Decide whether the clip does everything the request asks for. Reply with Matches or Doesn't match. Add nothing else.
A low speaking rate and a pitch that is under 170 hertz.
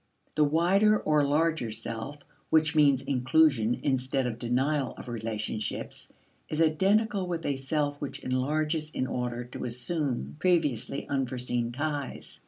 Matches